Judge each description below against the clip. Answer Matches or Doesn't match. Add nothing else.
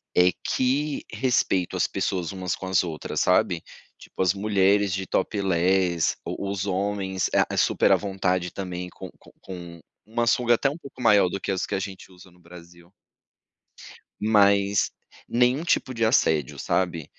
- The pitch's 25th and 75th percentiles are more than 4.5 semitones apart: Doesn't match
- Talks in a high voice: Doesn't match